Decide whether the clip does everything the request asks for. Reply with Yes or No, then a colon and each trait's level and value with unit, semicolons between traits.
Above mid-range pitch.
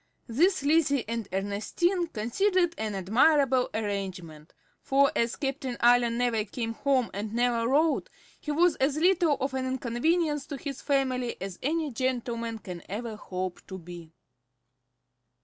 Yes: high, 245 Hz